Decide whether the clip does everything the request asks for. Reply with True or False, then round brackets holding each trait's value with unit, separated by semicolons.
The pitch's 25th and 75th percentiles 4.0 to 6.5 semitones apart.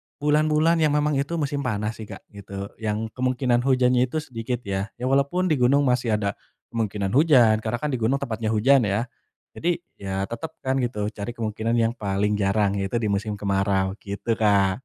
True (4.7 semitones)